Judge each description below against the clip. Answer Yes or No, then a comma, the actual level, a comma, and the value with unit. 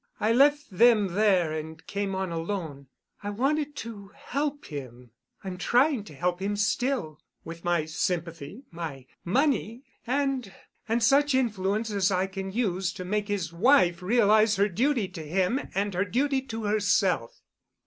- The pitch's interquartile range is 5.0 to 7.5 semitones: Yes, wide, 5.4 semitones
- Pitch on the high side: Yes, high, 200 Hz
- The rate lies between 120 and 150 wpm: Yes, average, 140 wpm